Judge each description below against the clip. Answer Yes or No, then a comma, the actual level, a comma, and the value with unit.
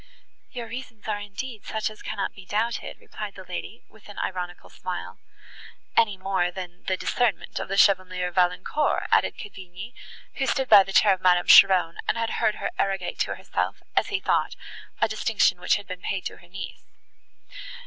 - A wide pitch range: No, average, 3.0 semitones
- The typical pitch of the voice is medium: No, high, 195 Hz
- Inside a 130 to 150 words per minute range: No, average, 180 wpm